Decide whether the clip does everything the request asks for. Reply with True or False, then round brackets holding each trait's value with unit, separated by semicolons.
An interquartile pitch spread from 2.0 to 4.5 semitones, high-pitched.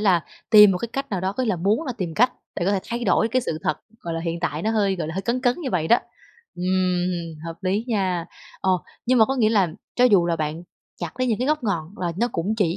False (5.2 semitones; 195 Hz)